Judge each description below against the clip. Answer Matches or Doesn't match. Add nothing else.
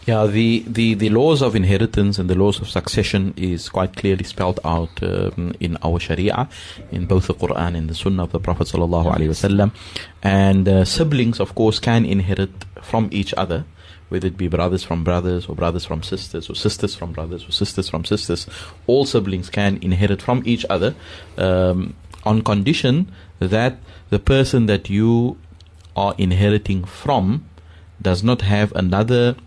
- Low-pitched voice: Matches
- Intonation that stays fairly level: Doesn't match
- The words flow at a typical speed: Matches